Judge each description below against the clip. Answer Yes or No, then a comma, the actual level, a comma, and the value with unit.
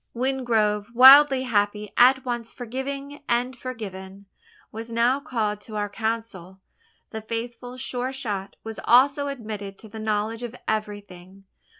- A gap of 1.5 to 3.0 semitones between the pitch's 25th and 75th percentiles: No, average, 3.5 semitones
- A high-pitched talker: Yes, high, 230 Hz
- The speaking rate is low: Yes, slow, 130 wpm